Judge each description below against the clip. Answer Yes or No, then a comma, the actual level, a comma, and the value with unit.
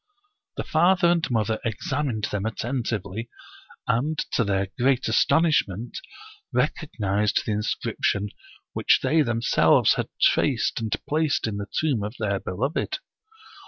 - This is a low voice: Yes, low, 115 Hz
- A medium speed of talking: No, slow, 125 wpm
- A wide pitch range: Yes, wide, 5.8 semitones